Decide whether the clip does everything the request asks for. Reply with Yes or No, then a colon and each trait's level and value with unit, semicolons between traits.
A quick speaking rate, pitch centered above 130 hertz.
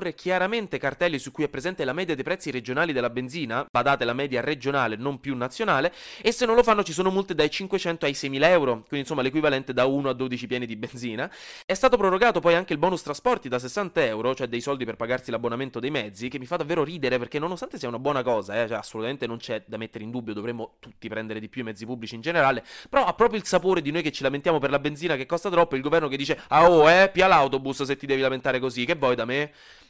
Yes: fast, 255 wpm; medium, 140 Hz